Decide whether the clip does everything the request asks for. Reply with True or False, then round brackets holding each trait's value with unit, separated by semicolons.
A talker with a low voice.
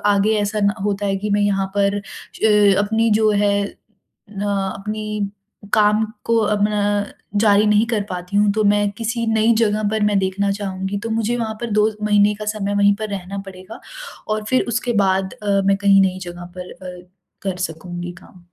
False (205 Hz)